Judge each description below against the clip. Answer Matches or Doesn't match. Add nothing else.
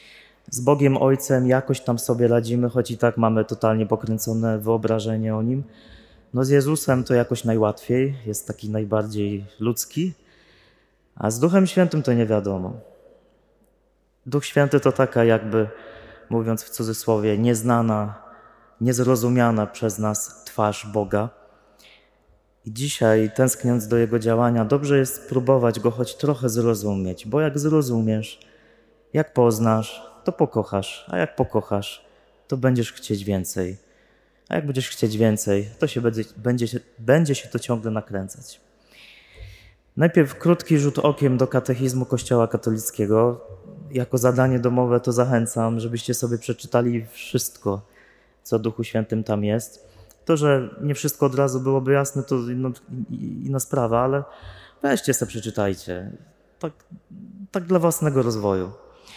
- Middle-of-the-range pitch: Doesn't match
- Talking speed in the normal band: Matches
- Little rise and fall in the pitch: Doesn't match